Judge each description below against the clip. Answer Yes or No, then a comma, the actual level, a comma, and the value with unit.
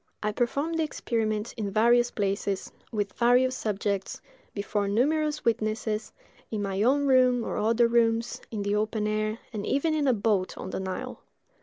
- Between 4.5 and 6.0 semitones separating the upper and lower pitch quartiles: No, average, 3.0 semitones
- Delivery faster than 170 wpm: No, average, 165 wpm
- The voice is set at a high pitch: Yes, high, 220 Hz